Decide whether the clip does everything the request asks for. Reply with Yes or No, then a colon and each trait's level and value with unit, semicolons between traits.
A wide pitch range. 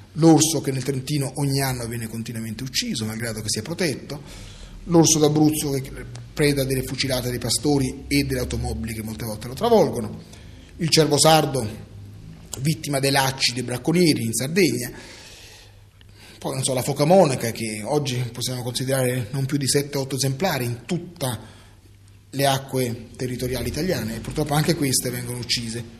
No: average, 3.9 semitones